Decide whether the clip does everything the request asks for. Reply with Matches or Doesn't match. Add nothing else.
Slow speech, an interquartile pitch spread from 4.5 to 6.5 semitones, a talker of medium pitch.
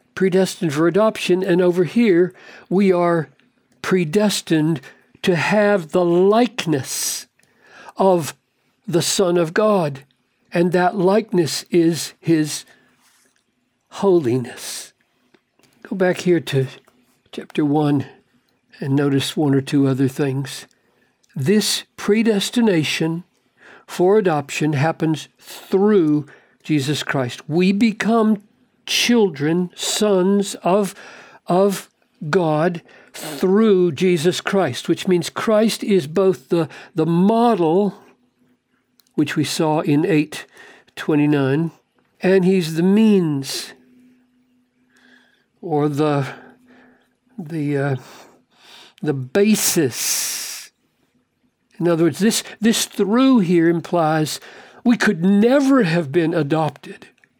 Matches